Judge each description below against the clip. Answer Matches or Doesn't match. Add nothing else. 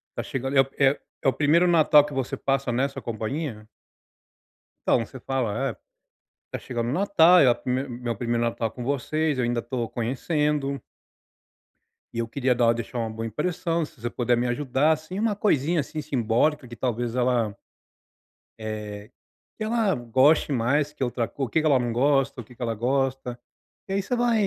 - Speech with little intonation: Doesn't match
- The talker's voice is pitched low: Matches